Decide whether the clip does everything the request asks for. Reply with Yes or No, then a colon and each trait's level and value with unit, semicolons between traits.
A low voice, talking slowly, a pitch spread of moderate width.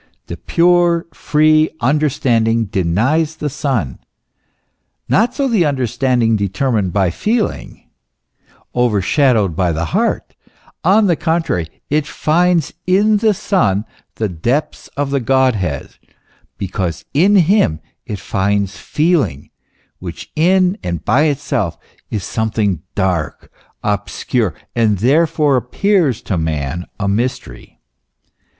No: low, 125 Hz; slow, 110 wpm; wide, 8.4 semitones